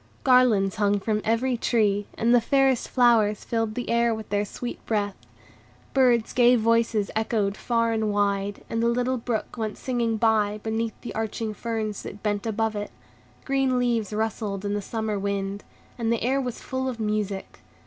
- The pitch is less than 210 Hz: No, high, 225 Hz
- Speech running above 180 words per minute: No, average, 175 wpm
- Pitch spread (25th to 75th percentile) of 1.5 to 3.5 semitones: Yes, narrow, 2.4 semitones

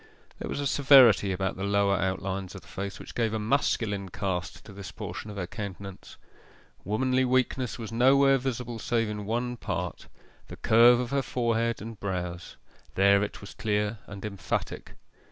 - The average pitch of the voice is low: Yes, low, 105 Hz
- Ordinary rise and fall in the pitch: Yes, average, 3.6 semitones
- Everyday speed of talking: Yes, average, 170 wpm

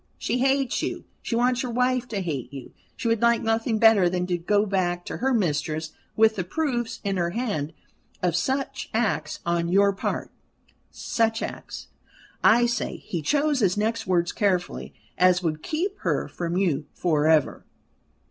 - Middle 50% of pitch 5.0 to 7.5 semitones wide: Yes, average, 5.3 semitones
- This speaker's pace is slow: No, average, 170 wpm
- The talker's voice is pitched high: Yes, high, 200 Hz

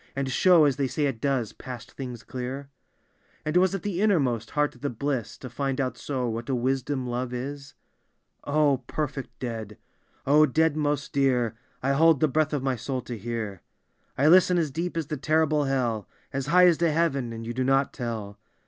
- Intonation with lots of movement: No, average, 3.6 semitones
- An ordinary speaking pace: No, fast, 215 wpm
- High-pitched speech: No, low, 135 Hz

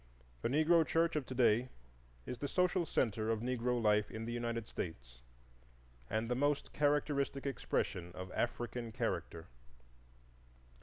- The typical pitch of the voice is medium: No, low, 120 Hz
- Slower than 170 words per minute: Yes, average, 140 wpm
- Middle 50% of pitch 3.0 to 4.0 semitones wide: No, average, 4.6 semitones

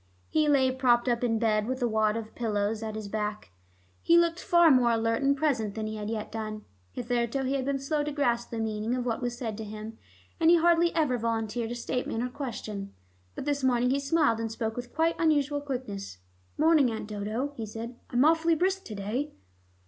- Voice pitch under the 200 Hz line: No, high, 240 Hz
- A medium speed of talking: No, fast, 215 wpm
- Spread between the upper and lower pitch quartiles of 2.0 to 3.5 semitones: No, average, 4.3 semitones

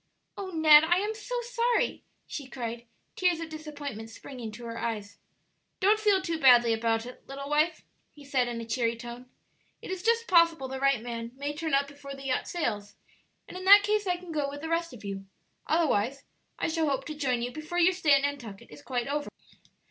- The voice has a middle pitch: No, very high, 285 Hz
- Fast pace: Yes, fast, 210 wpm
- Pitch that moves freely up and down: Yes, wide, 5.8 semitones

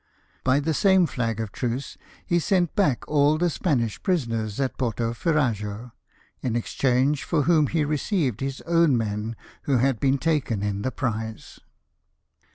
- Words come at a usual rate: Yes, average, 155 wpm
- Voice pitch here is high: No, low, 135 Hz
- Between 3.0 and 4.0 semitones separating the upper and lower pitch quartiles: No, average, 5.1 semitones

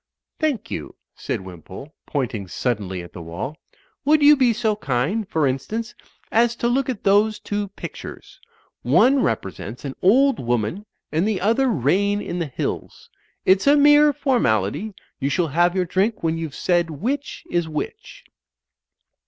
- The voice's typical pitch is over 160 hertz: Yes, high, 190 Hz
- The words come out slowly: No, average, 155 wpm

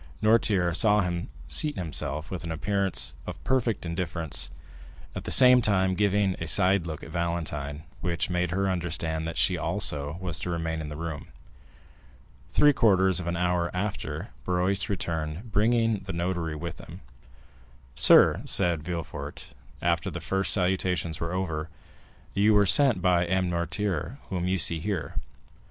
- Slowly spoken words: No, average, 155 wpm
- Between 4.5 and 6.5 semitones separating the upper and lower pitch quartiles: No, average, 2.8 semitones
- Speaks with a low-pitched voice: Yes, very low, 90 Hz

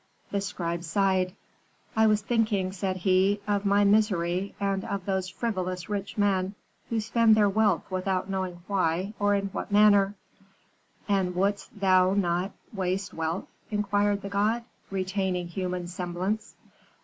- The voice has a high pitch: Yes, high, 195 Hz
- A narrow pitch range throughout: Yes, narrow, 1.8 semitones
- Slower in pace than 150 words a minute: Yes, average, 140 wpm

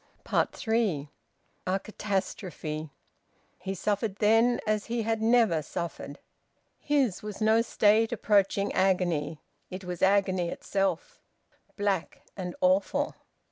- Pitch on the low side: No, high, 200 Hz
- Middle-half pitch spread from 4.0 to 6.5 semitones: No, average, 3.5 semitones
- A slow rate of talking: Yes, slow, 105 wpm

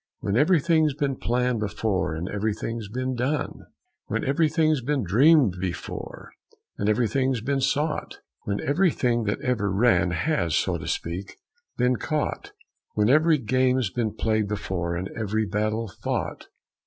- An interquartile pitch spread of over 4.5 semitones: Yes, average, 5.3 semitones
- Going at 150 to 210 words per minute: No, average, 140 wpm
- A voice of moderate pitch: No, low, 115 Hz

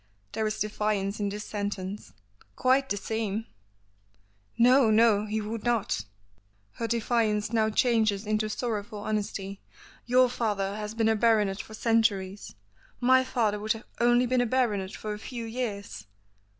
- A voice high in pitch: Yes, high, 215 Hz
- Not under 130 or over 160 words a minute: Yes, average, 150 wpm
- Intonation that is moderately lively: No, narrow, 2.2 semitones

